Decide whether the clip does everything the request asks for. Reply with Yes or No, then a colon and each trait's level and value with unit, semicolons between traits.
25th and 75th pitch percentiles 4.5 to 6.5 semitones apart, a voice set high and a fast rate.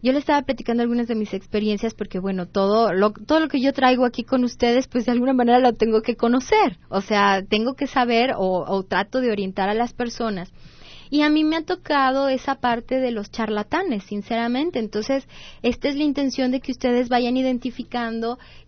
No: average, 3.4 semitones; high, 245 Hz; fast, 200 wpm